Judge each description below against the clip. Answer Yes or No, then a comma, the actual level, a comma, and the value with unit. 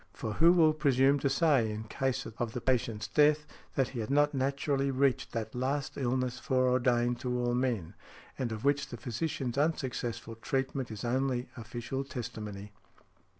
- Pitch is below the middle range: Yes, low, 130 Hz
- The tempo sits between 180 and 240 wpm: No, average, 160 wpm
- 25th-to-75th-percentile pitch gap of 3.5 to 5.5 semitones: No, narrow, 2.6 semitones